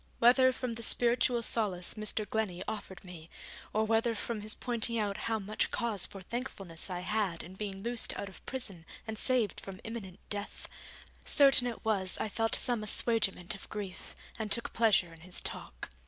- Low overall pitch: No, high, 215 Hz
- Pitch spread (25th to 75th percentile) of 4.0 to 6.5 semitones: No, average, 3.4 semitones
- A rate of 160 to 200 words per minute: Yes, average, 180 wpm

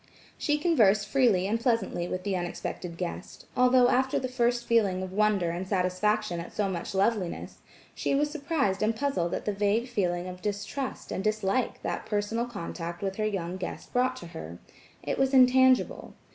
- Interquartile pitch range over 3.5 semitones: Yes, average, 5.2 semitones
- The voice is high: Yes, high, 210 Hz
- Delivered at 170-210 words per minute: Yes, average, 175 wpm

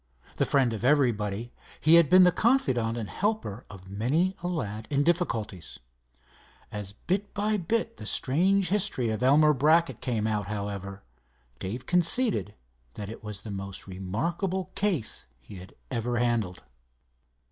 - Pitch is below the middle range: Yes, low, 125 Hz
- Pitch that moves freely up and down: Yes, wide, 9.0 semitones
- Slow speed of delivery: No, average, 145 wpm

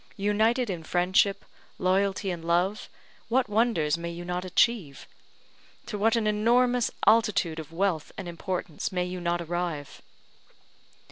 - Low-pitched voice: No, medium, 185 Hz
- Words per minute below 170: Yes, slow, 135 wpm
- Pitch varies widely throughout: No, average, 3.8 semitones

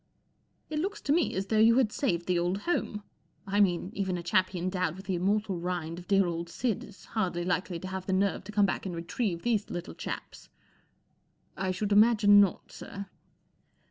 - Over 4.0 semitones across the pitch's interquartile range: No, average, 2.8 semitones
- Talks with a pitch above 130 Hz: Yes, high, 190 Hz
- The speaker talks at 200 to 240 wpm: Yes, fast, 205 wpm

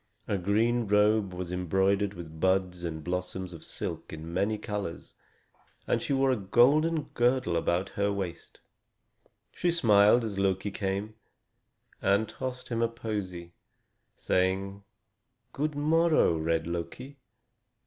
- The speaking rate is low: Yes, slow, 130 wpm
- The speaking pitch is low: Yes, low, 100 Hz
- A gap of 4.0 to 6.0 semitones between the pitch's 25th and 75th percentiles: Yes, average, 4.4 semitones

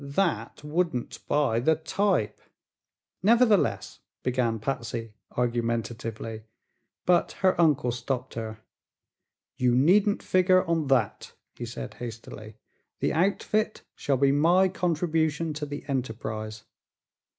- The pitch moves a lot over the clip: Yes, wide, 6.5 semitones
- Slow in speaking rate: Yes, slow, 105 wpm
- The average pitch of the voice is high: No, medium, 140 Hz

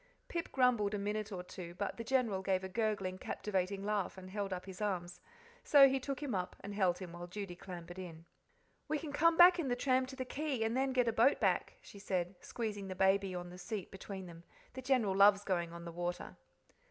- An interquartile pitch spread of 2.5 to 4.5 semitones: No, average, 5.3 semitones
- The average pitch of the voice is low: No, high, 200 Hz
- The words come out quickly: Yes, fast, 225 wpm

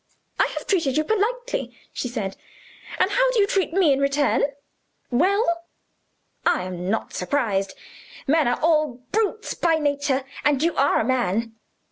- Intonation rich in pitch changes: Yes, wide, 6.8 semitones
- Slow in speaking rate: No, average, 155 wpm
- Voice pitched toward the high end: Yes, very high, 290 Hz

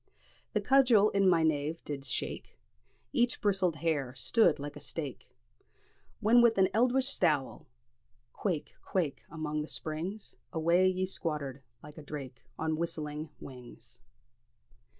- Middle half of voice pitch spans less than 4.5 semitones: No, average, 4.8 semitones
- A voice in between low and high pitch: Yes, medium, 160 Hz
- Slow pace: Yes, slow, 130 wpm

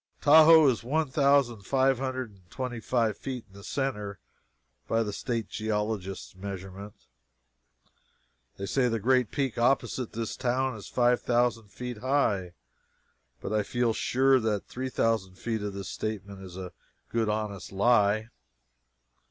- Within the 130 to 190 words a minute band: Yes, average, 150 wpm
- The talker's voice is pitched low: Yes, low, 115 Hz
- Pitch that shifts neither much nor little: Yes, average, 4.1 semitones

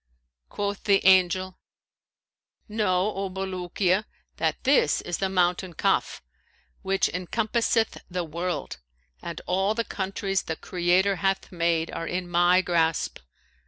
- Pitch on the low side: No, medium, 185 Hz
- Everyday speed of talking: No, slow, 125 wpm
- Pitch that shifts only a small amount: Yes, narrow, 1.8 semitones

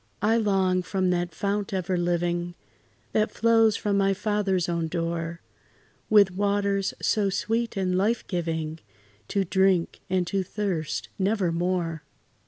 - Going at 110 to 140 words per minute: Yes, slow, 135 wpm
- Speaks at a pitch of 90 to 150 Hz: No, high, 190 Hz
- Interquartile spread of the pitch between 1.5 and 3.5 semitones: Yes, average, 2.7 semitones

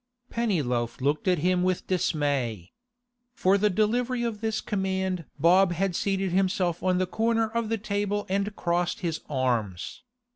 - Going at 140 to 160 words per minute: Yes, average, 150 wpm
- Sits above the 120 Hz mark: Yes, medium, 185 Hz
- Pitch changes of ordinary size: Yes, average, 4.1 semitones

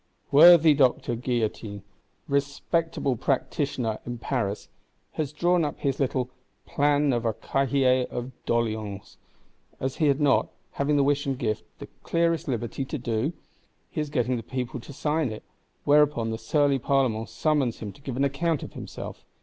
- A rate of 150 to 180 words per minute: Yes, average, 160 wpm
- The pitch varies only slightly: No, average, 3.6 semitones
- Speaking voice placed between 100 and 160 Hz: Yes, low, 135 Hz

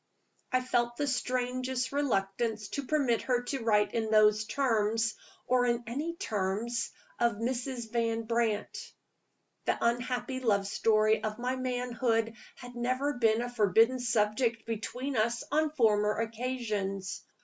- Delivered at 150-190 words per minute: No, slow, 135 wpm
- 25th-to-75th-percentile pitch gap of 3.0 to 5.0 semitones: No, narrow, 2.6 semitones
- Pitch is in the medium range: No, high, 235 Hz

